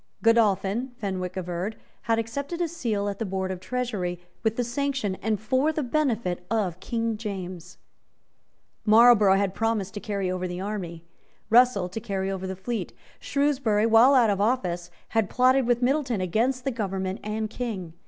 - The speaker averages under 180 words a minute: Yes, average, 165 wpm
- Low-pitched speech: No, high, 215 Hz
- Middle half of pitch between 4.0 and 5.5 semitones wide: Yes, average, 4.3 semitones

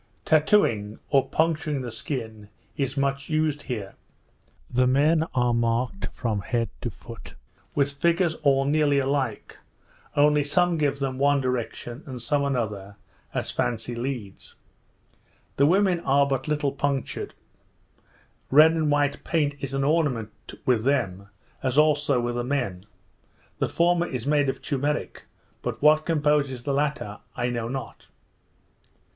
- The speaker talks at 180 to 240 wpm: No, average, 140 wpm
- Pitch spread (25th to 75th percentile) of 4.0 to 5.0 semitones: No, average, 3.5 semitones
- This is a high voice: No, medium, 140 Hz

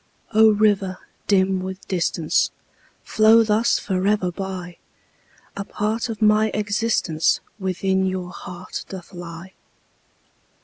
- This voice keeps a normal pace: No, slow, 105 wpm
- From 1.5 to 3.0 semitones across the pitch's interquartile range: Yes, narrow, 2.5 semitones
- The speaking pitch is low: No, high, 190 Hz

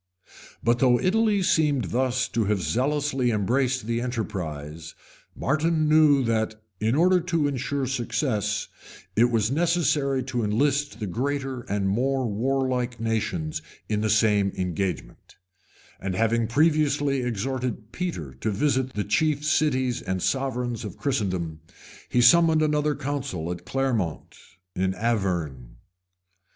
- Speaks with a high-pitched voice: No, low, 125 Hz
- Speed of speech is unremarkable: No, slow, 125 wpm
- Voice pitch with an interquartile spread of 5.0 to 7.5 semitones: Yes, average, 5.3 semitones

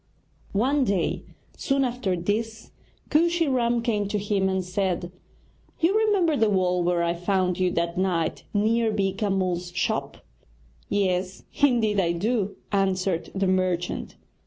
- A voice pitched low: No, high, 195 Hz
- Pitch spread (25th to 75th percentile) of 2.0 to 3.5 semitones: No, average, 4.1 semitones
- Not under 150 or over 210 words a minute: No, slow, 135 wpm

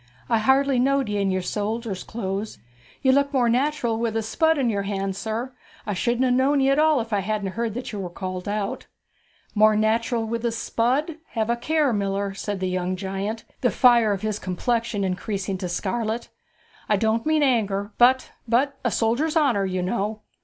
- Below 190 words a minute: No, average, 195 wpm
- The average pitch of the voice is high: Yes, high, 225 Hz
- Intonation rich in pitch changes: No, average, 3.9 semitones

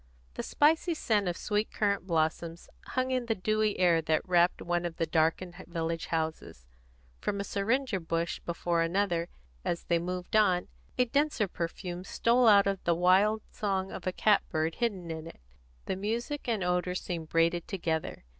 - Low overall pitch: No, medium, 180 Hz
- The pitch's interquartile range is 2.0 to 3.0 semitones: No, average, 4.0 semitones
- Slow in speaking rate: No, average, 175 wpm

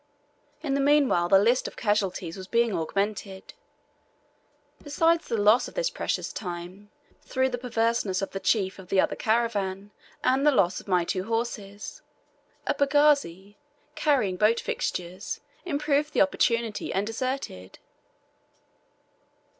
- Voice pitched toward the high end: Yes, high, 215 Hz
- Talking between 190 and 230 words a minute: No, slow, 135 wpm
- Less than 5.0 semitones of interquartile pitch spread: No, wide, 5.6 semitones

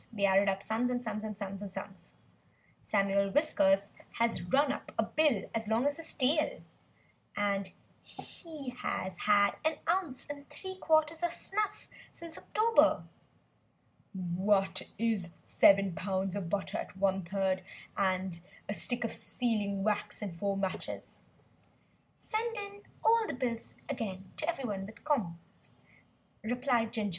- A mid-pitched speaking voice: No, high, 220 Hz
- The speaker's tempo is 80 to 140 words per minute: Yes, slow, 135 wpm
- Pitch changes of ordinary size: No, wide, 6.8 semitones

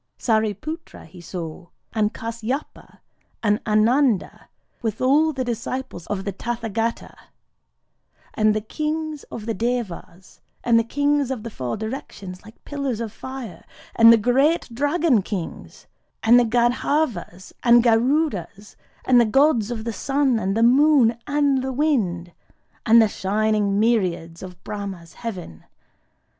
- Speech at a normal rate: No, slow, 125 wpm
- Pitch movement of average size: Yes, average, 4.3 semitones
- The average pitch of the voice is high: Yes, high, 230 Hz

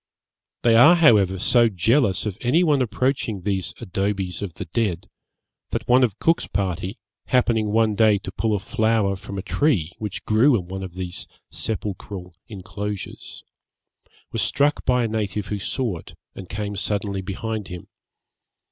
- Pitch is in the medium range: No, low, 105 Hz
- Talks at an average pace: Yes, average, 160 wpm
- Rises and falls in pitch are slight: No, average, 3.3 semitones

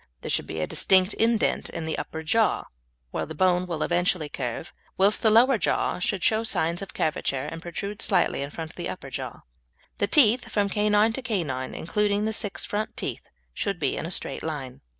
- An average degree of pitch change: Yes, average, 4.9 semitones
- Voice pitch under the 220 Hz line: Yes, medium, 185 Hz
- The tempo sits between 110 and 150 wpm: No, fast, 205 wpm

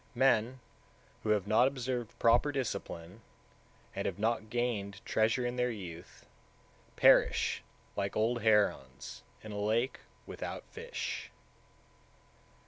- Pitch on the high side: No, low, 110 Hz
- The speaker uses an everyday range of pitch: Yes, average, 3.1 semitones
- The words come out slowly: Yes, slow, 120 wpm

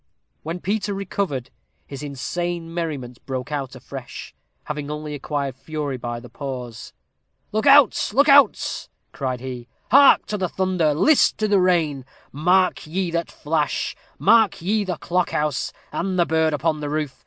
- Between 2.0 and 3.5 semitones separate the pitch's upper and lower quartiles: No, average, 5.2 semitones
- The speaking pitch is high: No, medium, 155 Hz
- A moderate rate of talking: Yes, average, 155 wpm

